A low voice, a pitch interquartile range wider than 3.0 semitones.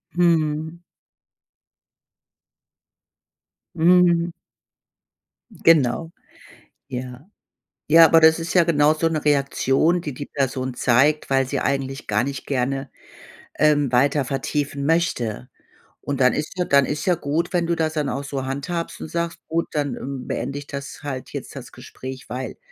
No: medium, 145 Hz; average, 3.5 semitones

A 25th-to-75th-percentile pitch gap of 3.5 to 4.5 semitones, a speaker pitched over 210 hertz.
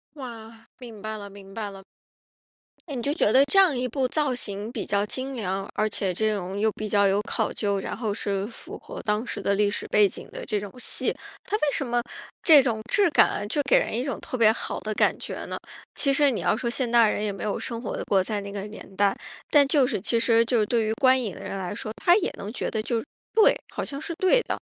Yes: average, 4.0 semitones; high, 220 Hz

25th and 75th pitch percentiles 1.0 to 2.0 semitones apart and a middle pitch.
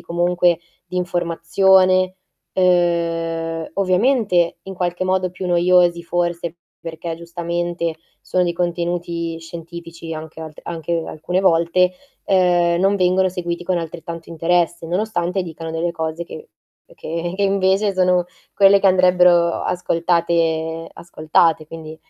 Yes: narrow, 1.5 semitones; medium, 175 Hz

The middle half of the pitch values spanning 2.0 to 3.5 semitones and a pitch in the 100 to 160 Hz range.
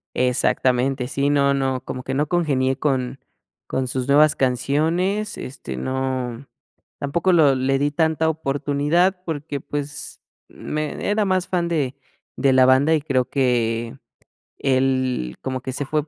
Yes: average, 2.8 semitones; medium, 140 Hz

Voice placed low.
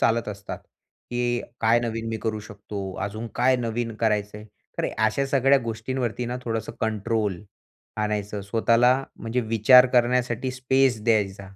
Yes: low, 115 Hz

